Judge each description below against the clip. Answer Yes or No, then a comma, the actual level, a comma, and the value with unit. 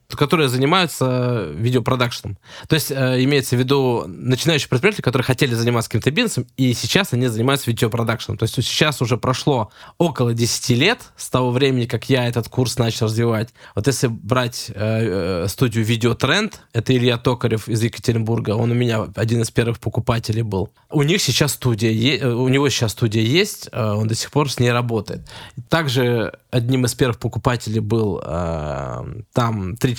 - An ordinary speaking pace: No, fast, 170 wpm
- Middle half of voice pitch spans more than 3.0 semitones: No, narrow, 2.4 semitones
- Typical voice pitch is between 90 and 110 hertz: No, low, 120 Hz